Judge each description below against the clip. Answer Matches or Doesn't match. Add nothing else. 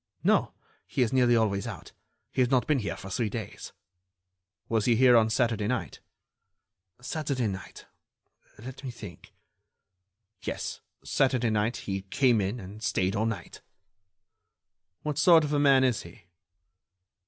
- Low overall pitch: Matches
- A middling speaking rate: Matches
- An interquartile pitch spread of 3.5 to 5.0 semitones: Matches